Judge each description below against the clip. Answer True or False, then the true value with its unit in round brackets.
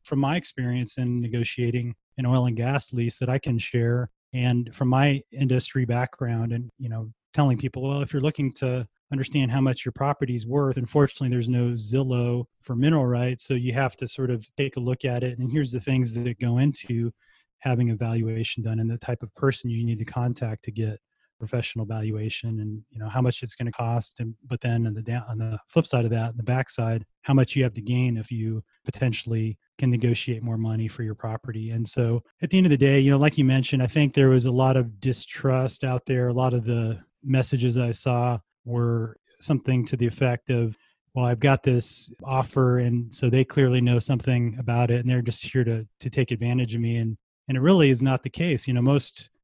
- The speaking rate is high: True (225 wpm)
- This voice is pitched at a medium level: False (125 Hz)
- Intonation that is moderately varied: False (2.1 semitones)